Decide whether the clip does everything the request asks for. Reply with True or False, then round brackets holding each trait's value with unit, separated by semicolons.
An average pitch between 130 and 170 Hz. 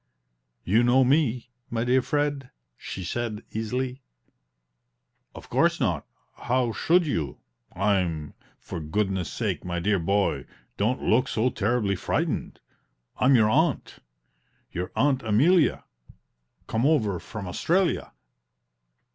False (115 Hz)